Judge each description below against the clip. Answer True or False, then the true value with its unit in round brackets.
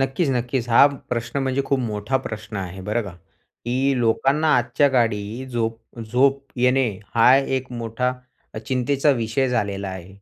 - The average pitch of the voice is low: True (120 Hz)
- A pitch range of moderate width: True (3.1 semitones)